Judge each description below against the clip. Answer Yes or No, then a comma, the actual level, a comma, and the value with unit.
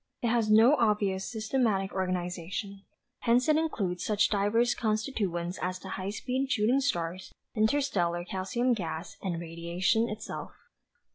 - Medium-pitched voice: No, high, 205 Hz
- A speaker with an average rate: No, slow, 130 wpm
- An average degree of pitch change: Yes, average, 4.2 semitones